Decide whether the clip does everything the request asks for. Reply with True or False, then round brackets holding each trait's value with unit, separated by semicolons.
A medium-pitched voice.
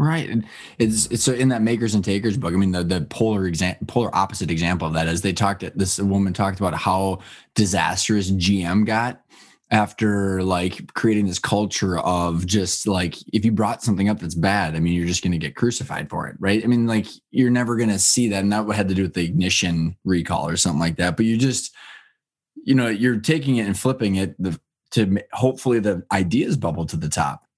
False (100 Hz)